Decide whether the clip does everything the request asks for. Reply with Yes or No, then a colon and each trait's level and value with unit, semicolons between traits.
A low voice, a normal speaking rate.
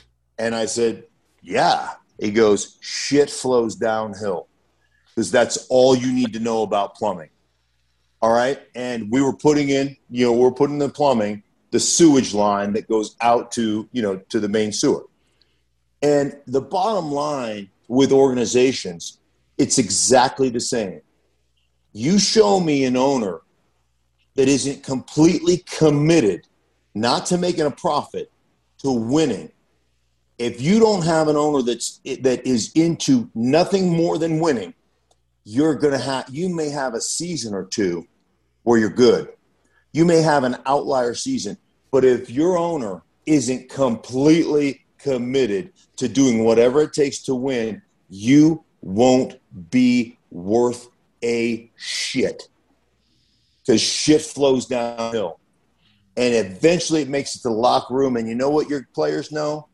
Yes: low, 130 Hz; average, 145 wpm